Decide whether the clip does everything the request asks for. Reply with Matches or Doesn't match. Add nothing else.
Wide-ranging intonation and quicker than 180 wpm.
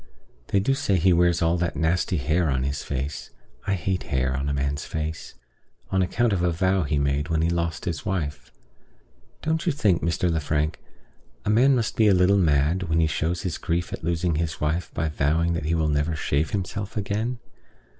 Doesn't match